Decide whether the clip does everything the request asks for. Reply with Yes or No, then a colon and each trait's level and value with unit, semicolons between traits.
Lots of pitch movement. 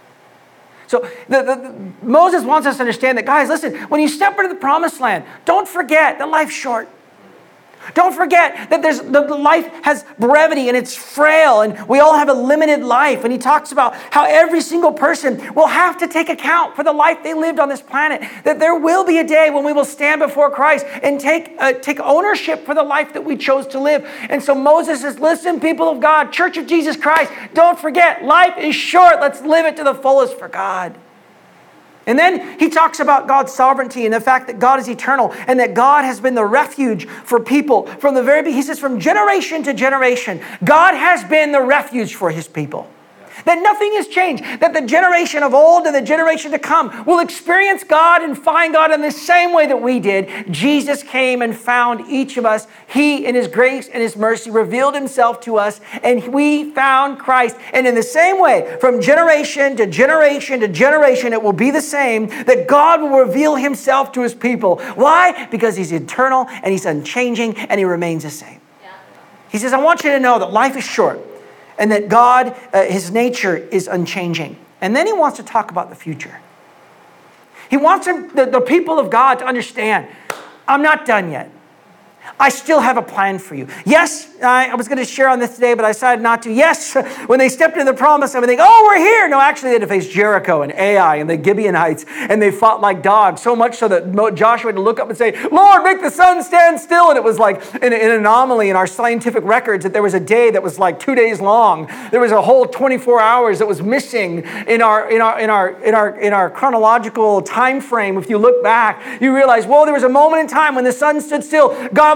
No: average, 5.0 semitones